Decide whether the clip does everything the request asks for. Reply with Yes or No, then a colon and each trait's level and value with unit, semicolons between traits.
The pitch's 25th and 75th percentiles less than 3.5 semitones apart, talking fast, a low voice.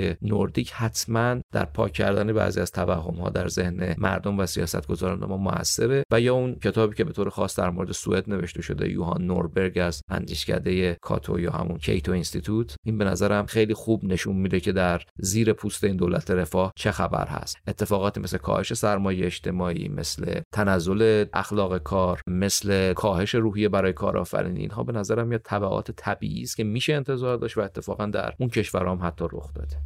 Yes: average, 2.9 semitones; fast, 180 wpm; very low, 95 Hz